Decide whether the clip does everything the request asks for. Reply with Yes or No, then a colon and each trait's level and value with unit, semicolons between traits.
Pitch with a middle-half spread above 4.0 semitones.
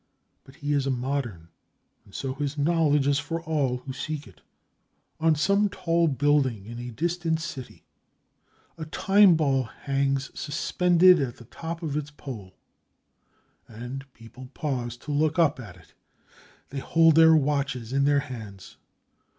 No: average, 3.7 semitones